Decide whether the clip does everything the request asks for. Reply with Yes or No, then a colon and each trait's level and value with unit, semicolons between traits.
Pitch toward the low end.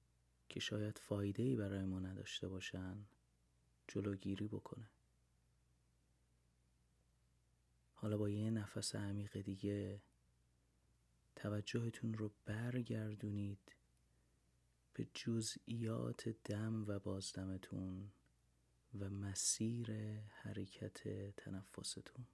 Yes: low, 100 Hz